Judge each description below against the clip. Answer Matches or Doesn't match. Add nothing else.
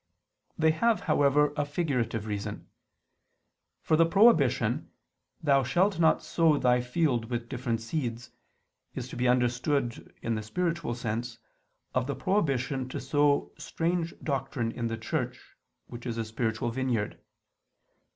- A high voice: Doesn't match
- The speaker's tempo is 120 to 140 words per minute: Matches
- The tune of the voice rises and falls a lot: Doesn't match